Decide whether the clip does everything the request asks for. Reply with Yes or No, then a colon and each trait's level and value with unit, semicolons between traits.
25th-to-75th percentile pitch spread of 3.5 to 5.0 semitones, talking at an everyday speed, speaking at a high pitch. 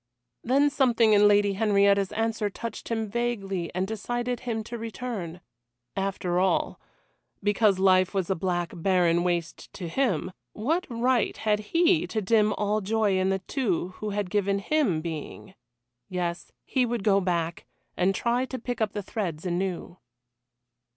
Yes: average, 3.8 semitones; average, 155 wpm; high, 205 Hz